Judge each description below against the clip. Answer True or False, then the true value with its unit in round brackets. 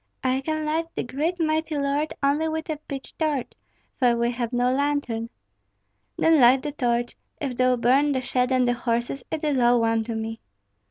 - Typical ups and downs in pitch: True (3.7 semitones)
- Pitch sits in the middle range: False (260 Hz)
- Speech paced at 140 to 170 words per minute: False (195 wpm)